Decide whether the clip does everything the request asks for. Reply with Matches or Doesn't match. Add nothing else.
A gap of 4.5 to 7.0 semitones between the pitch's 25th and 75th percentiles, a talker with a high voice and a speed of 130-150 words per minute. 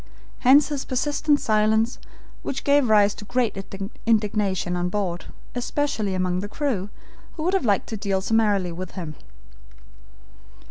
Matches